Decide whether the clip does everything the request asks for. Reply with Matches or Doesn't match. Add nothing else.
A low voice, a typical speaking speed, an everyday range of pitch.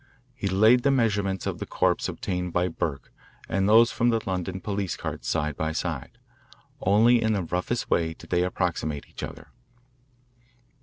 Matches